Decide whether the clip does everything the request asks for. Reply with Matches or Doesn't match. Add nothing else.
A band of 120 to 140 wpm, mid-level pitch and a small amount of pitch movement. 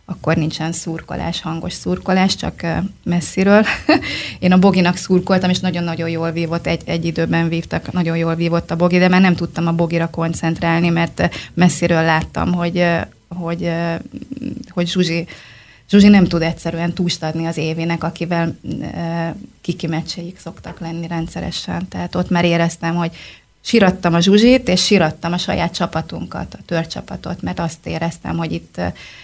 Doesn't match